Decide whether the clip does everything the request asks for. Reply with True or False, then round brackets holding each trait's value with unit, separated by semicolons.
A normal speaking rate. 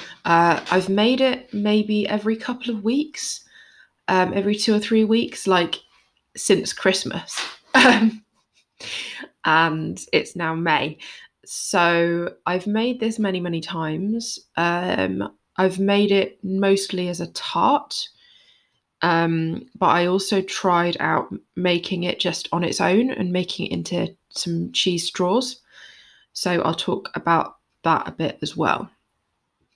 False (130 wpm)